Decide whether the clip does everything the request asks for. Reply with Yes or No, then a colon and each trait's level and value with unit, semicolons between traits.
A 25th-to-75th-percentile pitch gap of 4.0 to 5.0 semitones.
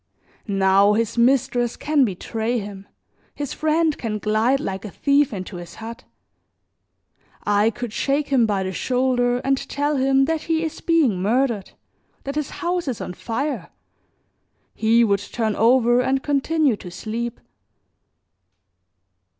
Yes: average, 4.7 semitones